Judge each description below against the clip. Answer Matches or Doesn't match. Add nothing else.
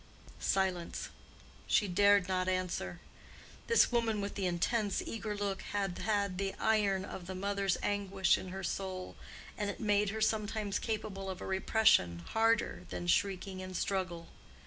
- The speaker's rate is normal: Matches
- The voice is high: Matches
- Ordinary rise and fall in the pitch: Doesn't match